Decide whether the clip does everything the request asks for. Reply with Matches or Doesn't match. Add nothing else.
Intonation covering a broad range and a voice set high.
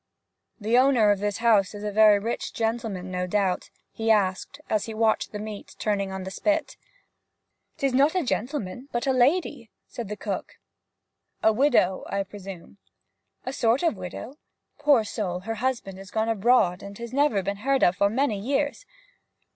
Doesn't match